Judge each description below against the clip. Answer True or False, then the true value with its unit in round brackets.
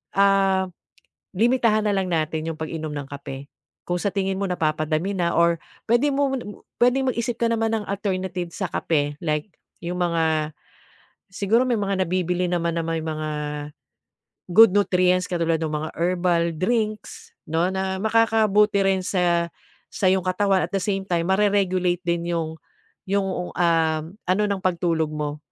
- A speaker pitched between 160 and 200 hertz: True (185 Hz)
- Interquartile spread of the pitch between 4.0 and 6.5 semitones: False (3.3 semitones)